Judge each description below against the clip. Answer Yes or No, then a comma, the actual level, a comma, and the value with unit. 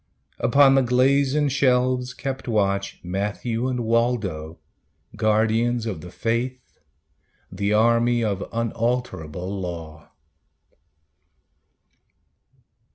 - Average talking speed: No, slow, 85 wpm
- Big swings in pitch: No, average, 4.2 semitones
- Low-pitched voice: Yes, low, 115 Hz